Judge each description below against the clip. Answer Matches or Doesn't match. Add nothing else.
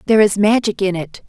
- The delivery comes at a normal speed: Doesn't match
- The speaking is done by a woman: Matches